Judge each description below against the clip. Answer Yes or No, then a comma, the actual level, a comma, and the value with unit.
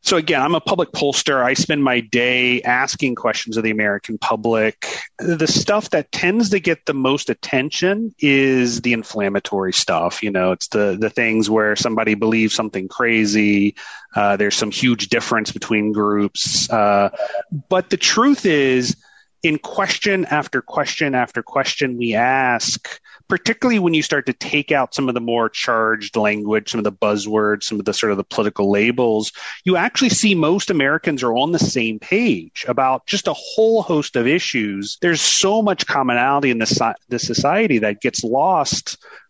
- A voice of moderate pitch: No, low, 125 Hz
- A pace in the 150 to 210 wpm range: Yes, average, 170 wpm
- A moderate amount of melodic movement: No, wide, 6.7 semitones